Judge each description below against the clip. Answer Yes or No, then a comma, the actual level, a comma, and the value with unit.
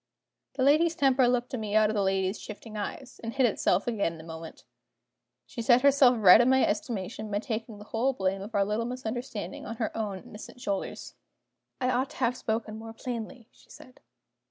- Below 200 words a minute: No, fast, 205 wpm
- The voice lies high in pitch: Yes, high, 225 Hz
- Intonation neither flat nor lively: Yes, average, 3.5 semitones